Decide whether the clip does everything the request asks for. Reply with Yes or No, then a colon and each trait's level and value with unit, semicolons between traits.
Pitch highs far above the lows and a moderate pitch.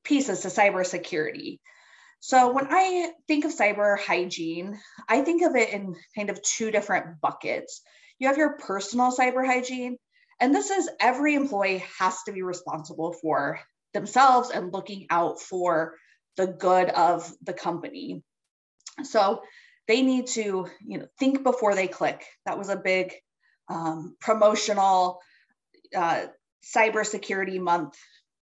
No: wide, 5.8 semitones; high, 210 Hz